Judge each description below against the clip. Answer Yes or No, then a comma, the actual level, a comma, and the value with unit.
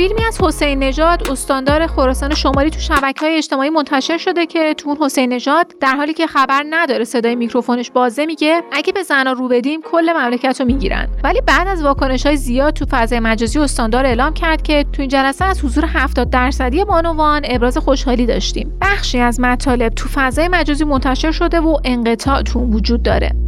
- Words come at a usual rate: No, fast, 185 wpm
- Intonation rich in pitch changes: No, average, 3.8 semitones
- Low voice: No, very high, 280 Hz